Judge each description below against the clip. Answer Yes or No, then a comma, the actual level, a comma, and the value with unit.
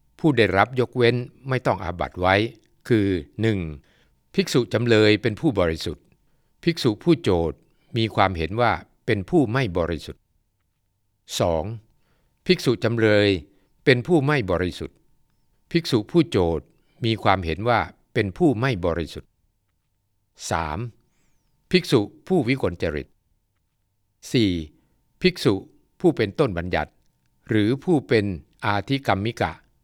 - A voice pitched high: No, low, 110 Hz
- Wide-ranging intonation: Yes, wide, 6.1 semitones